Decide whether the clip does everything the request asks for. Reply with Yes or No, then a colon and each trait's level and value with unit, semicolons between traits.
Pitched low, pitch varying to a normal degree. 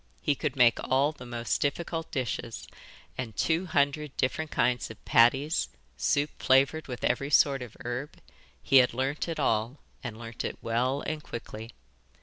Yes: low, 130 Hz; average, 3.6 semitones